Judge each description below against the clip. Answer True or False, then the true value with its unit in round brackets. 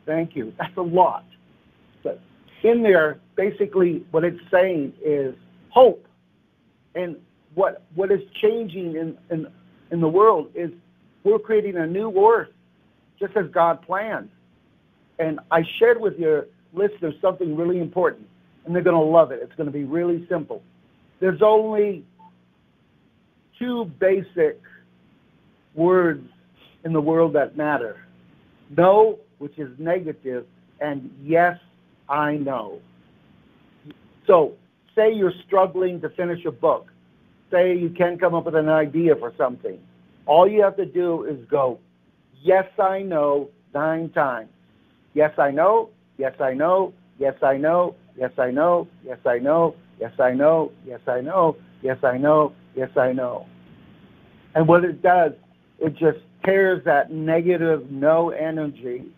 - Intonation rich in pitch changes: False (4.8 semitones)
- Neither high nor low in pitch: True (165 Hz)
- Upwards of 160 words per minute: False (140 wpm)